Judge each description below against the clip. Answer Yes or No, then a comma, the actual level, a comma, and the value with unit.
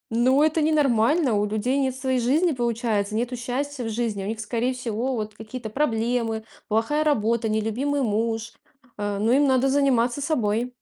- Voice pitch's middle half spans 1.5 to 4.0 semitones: Yes, average, 3.4 semitones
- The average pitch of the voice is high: Yes, high, 240 Hz